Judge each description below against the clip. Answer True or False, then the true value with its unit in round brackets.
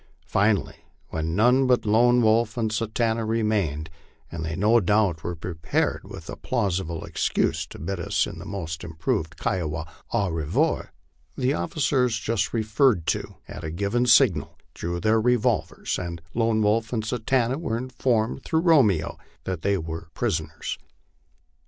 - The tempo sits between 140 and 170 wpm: True (150 wpm)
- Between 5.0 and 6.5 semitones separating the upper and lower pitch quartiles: True (5.5 semitones)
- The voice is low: True (105 Hz)